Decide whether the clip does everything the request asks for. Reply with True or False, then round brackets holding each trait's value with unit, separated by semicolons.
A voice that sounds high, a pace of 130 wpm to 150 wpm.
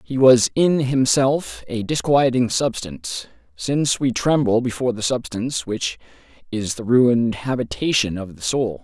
False (120 Hz; 145 wpm)